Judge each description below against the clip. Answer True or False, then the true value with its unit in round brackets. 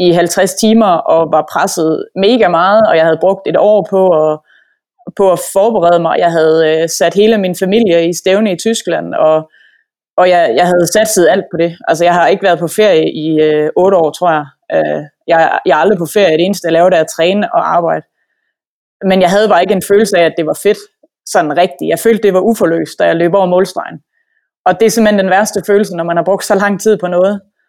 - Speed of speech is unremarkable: False (235 wpm)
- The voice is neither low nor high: True (180 Hz)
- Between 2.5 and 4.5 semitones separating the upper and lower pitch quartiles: True (3.6 semitones)